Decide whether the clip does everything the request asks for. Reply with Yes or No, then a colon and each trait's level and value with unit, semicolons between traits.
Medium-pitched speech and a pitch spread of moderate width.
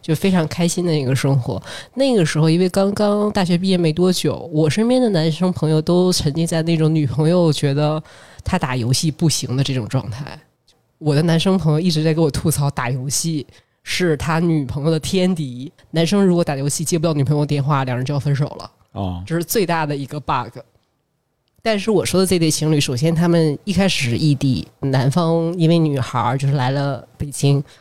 Yes: medium, 155 Hz; average, 3.6 semitones